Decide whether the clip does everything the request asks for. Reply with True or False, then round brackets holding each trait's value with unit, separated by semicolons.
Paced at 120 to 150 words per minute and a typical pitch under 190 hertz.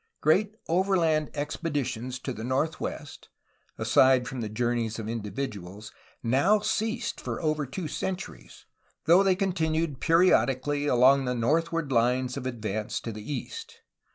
True (140 wpm; 140 Hz)